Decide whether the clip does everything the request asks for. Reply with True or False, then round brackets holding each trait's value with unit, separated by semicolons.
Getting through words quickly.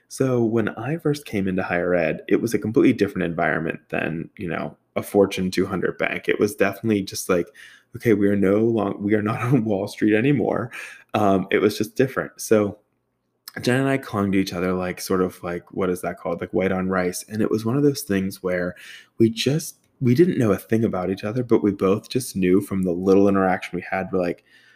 True (230 wpm)